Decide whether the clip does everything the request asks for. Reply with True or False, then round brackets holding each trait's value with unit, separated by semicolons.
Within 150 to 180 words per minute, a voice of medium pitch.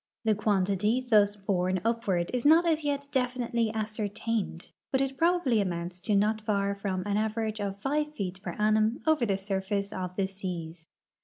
False (170 wpm; 210 Hz)